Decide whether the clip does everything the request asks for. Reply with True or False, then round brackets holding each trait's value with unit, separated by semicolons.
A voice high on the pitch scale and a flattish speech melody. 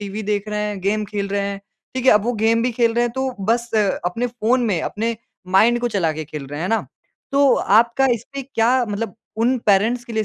False (220 Hz; 3.0 semitones)